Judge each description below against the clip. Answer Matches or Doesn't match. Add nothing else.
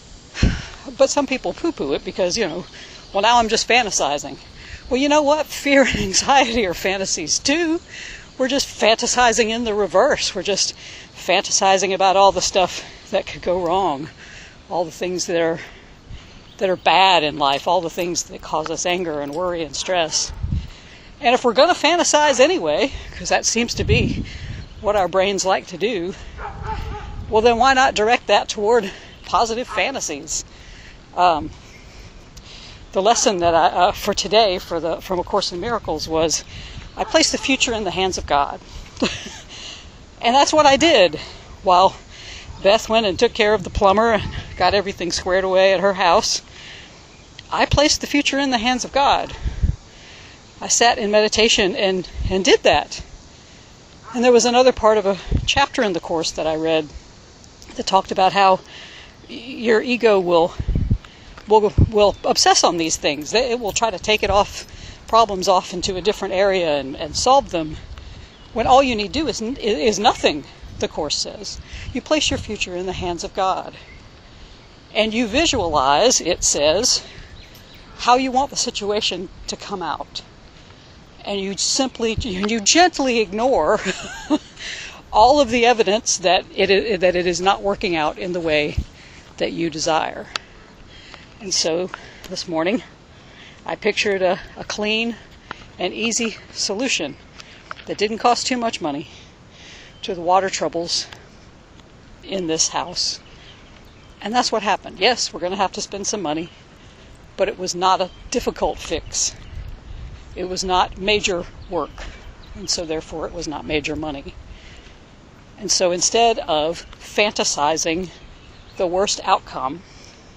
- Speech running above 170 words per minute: Doesn't match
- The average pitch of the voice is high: Matches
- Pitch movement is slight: Doesn't match